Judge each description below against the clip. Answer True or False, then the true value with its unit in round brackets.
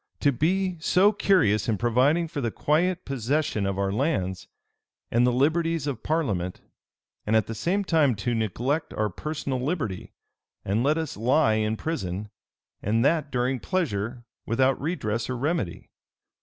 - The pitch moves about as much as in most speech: False (6.5 semitones)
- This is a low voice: True (130 Hz)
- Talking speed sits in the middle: True (155 wpm)